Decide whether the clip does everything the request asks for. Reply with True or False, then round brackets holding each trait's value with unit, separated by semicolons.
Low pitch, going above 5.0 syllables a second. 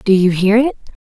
False (210 Hz; 5.7 syllables/s)